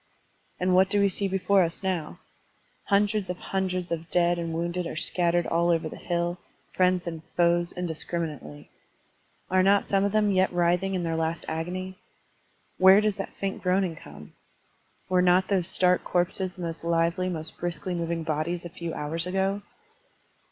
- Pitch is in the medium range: Yes, medium, 175 Hz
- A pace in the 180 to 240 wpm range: No, average, 170 wpm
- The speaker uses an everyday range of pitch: No, narrow, 2.0 semitones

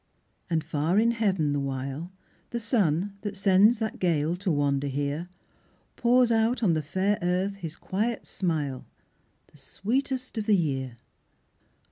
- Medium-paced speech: Yes, average, 145 wpm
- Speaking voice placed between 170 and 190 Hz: Yes, medium, 185 Hz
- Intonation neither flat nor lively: No, wide, 6.6 semitones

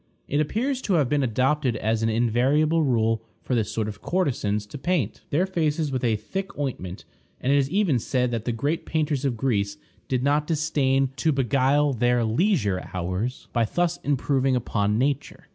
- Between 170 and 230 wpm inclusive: Yes, average, 180 wpm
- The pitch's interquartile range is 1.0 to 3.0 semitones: No, average, 4.8 semitones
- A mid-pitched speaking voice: No, low, 130 Hz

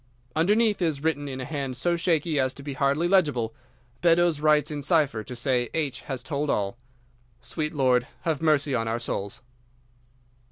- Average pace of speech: Yes, average, 170 wpm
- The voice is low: No, medium, 145 Hz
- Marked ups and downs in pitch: No, average, 3.9 semitones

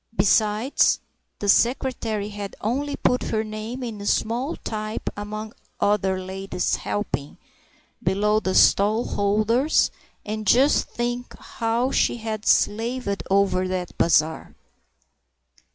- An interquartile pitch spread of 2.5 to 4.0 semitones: Yes, average, 2.9 semitones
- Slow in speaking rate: Yes, slow, 105 wpm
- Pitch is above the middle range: Yes, high, 215 Hz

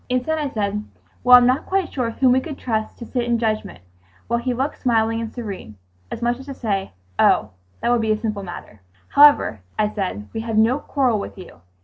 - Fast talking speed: Yes, fast, 215 wpm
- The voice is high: Yes, high, 230 Hz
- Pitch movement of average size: Yes, average, 3.4 semitones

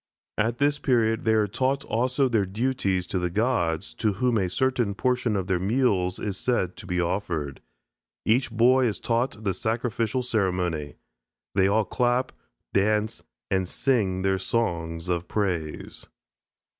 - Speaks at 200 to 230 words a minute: No, average, 150 wpm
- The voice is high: No, low, 105 Hz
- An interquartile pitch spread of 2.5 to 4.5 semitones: No, average, 4.9 semitones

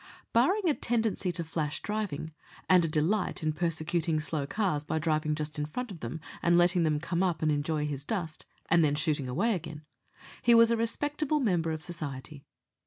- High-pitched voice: No, medium, 165 Hz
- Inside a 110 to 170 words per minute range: No, average, 190 wpm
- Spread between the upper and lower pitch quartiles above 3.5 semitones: Yes, average, 5.1 semitones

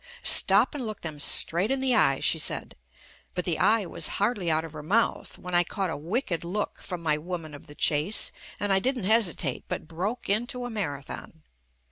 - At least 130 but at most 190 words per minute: No, fast, 205 wpm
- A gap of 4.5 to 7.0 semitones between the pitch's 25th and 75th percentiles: Yes, average, 5.3 semitones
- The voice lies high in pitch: No, medium, 180 Hz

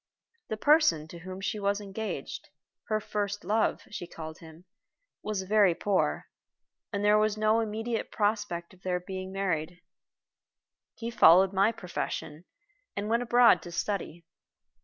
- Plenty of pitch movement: No, average, 3.4 semitones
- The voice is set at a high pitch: Yes, high, 200 Hz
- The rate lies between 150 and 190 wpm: No, average, 140 wpm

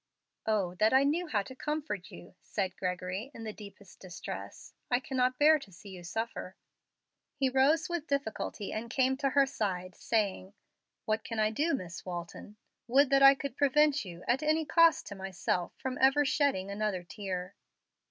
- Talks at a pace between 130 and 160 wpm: No, average, 175 wpm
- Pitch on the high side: Yes, high, 225 Hz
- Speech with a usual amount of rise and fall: No, wide, 6.4 semitones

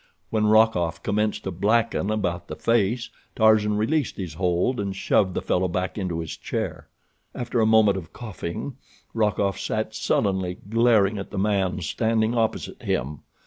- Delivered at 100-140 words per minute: No, average, 155 wpm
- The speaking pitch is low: Yes, low, 105 Hz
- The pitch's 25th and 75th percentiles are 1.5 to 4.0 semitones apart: Yes, average, 3.1 semitones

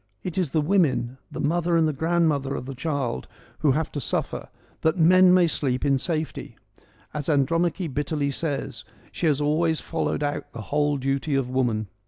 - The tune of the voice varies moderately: Yes, average, 3.2 semitones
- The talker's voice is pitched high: No, medium, 150 Hz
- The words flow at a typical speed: Yes, average, 175 wpm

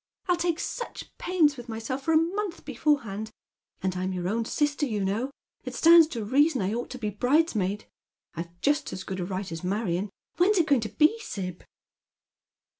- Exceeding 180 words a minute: Yes, average, 195 wpm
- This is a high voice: Yes, high, 240 Hz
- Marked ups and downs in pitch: Yes, wide, 8.3 semitones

